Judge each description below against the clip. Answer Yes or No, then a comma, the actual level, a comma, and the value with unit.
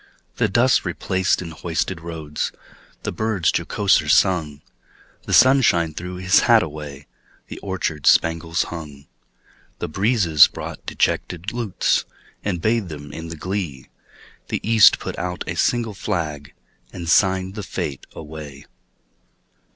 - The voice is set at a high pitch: No, very low, 85 Hz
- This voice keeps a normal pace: No, slow, 130 wpm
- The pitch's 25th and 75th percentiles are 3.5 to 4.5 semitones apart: Yes, average, 3.9 semitones